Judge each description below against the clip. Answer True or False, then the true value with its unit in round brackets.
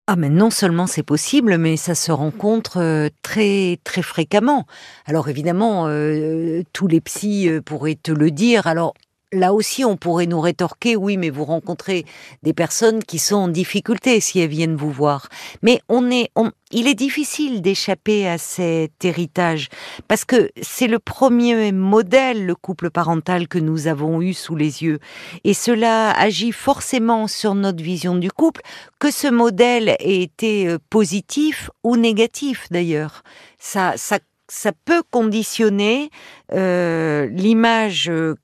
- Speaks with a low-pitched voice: False (190 Hz)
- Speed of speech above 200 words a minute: False (155 wpm)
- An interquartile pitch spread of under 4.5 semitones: False (5.4 semitones)